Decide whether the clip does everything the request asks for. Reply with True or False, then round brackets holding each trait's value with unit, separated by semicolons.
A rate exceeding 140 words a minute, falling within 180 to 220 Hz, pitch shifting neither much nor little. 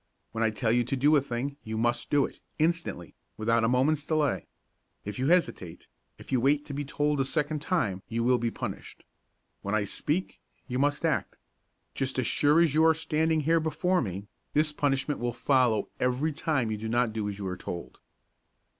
False (200 wpm; 135 Hz; 5.0 semitones)